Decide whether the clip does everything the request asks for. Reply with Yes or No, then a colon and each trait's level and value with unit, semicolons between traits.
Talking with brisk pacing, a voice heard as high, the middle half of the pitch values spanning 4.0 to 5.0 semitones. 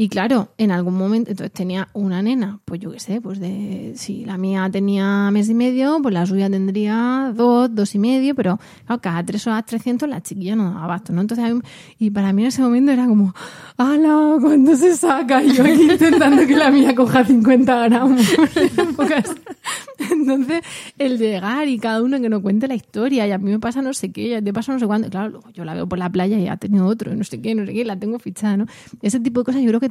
Yes: fast, 240 wpm; high, 230 Hz; average, 4.7 semitones